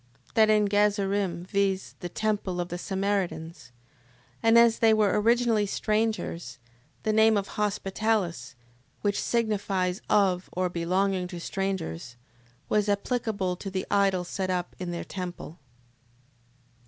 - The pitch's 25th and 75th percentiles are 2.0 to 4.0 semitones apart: Yes, average, 2.9 semitones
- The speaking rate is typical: No, slow, 130 wpm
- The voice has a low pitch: No, high, 195 Hz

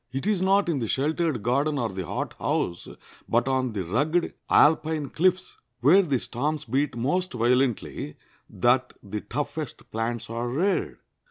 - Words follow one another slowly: No, average, 150 wpm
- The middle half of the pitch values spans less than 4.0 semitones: No, average, 4.9 semitones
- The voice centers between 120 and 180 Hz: Yes, low, 135 Hz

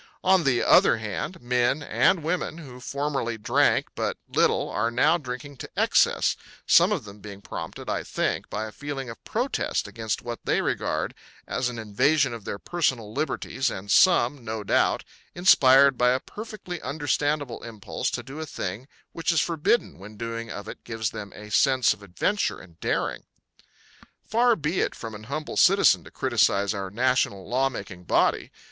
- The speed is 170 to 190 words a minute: Yes, average, 175 wpm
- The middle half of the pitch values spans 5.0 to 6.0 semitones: Yes, wide, 5.5 semitones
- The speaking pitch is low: Yes, low, 125 Hz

